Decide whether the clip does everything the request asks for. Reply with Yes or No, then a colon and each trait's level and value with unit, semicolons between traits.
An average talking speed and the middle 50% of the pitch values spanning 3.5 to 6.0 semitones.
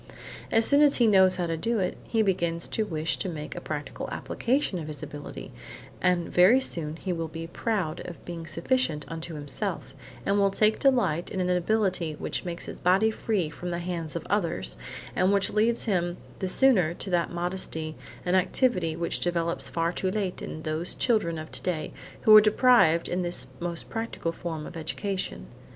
Yes: average, 190 wpm; average, 3.8 semitones